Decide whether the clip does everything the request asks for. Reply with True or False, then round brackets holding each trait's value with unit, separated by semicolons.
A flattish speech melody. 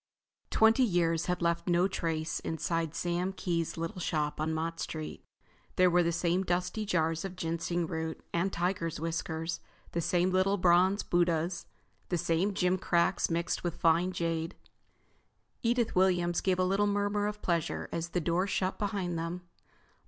True (2.0 semitones)